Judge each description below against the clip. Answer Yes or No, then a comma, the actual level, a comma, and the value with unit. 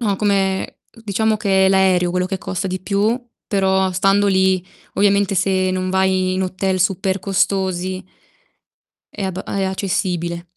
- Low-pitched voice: No, high, 190 Hz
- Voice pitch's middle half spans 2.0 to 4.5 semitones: No, narrow, 1.0 semitones